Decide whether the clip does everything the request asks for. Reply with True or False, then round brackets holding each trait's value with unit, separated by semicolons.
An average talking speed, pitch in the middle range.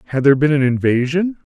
True (195 wpm; 145 Hz)